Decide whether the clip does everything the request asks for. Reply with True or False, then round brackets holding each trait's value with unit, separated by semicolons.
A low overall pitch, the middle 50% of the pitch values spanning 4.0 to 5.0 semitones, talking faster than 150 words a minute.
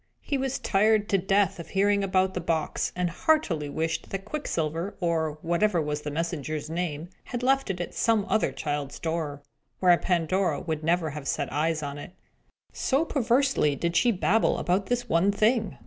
False (175 Hz; 4.6 semitones; 180 wpm)